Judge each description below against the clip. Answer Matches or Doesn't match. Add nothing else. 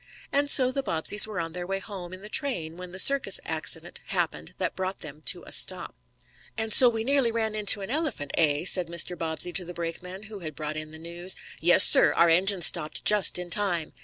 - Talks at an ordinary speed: Doesn't match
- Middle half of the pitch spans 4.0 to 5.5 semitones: Matches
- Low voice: Doesn't match